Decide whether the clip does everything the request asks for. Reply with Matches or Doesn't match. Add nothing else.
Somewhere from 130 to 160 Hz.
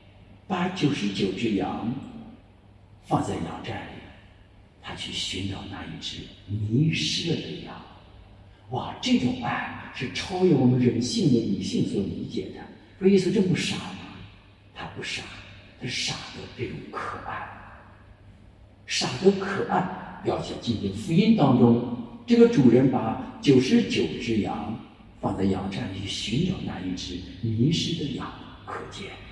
Doesn't match